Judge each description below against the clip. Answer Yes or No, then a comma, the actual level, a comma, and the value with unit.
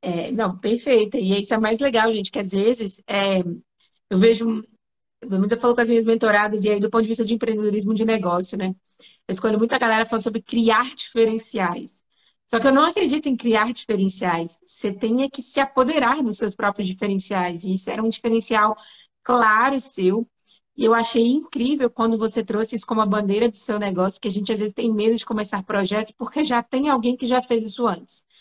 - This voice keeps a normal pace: No, fast, 205 wpm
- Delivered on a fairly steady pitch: Yes, narrow, 2.1 semitones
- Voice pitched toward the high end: Yes, high, 225 Hz